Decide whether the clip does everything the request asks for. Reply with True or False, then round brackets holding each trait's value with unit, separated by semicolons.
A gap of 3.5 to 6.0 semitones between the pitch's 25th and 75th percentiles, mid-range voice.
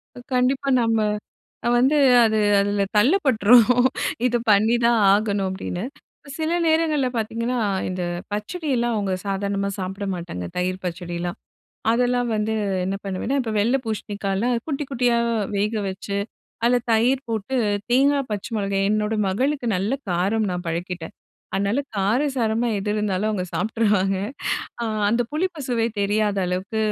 False (4.0 semitones; 215 Hz)